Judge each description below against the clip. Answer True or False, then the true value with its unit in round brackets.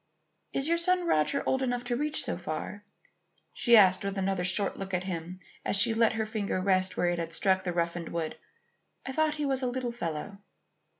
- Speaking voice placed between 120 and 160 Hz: False (200 Hz)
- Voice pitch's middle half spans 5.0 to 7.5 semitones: True (5.5 semitones)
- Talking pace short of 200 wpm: False (205 wpm)